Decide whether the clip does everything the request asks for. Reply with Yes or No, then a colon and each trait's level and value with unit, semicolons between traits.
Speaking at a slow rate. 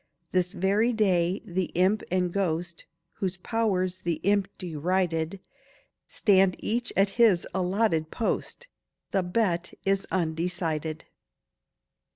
Yes: slow, 110 wpm